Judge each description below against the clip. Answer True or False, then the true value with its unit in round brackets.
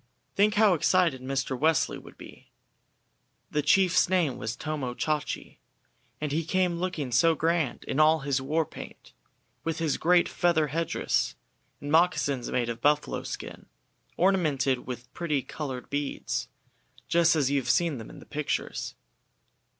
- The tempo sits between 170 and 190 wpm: False (150 wpm)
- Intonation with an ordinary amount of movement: True (3.8 semitones)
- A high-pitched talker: False (155 Hz)